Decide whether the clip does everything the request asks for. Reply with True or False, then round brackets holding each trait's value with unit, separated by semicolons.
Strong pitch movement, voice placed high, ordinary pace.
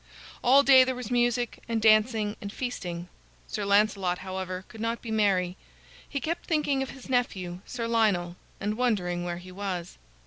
False (4.9 semitones; 215 Hz; 170 wpm)